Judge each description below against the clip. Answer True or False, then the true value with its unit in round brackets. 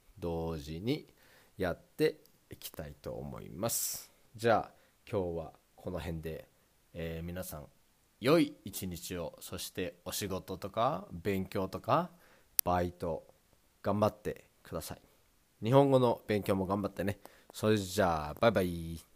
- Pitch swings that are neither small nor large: True (3.7 semitones)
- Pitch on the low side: True (95 Hz)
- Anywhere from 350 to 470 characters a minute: False (250 characters per minute)